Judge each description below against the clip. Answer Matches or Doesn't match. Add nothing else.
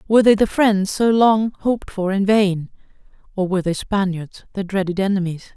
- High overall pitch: Matches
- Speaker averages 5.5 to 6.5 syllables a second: Doesn't match